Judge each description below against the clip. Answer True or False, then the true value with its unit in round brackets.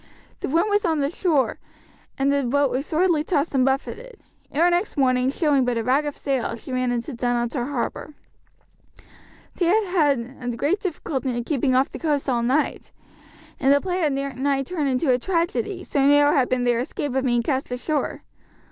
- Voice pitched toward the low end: False (275 Hz)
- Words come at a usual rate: True (190 wpm)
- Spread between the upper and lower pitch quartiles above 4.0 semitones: False (3.7 semitones)